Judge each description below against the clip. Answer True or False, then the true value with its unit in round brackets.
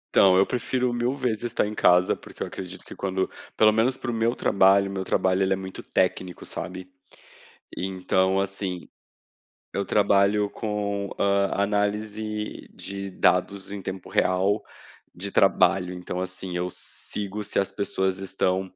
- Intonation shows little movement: True (1.9 semitones)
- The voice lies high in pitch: False (100 Hz)